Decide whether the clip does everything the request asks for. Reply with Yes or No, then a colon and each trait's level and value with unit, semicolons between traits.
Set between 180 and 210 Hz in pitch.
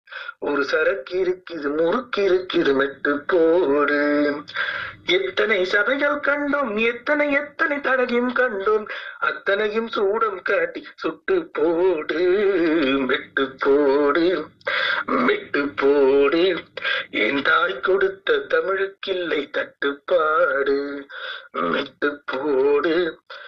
No: very high, 255 Hz